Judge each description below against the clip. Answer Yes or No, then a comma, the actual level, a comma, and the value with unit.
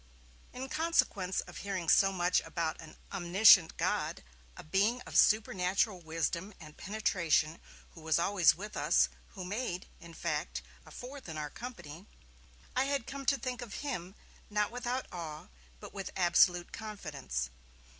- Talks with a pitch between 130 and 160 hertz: No, high, 190 Hz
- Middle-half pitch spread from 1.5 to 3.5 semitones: No, average, 4.8 semitones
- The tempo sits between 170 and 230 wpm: No, average, 150 wpm